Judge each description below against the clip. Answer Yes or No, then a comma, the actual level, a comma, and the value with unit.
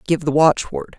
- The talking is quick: No, average, 185 wpm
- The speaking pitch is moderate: Yes, medium, 155 Hz